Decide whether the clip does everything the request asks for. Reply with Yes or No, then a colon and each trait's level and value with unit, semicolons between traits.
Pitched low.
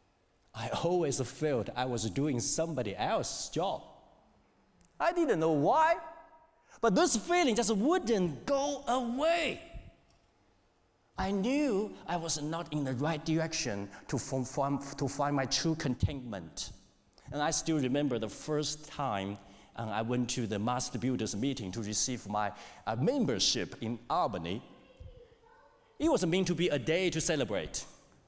No: medium, 150 Hz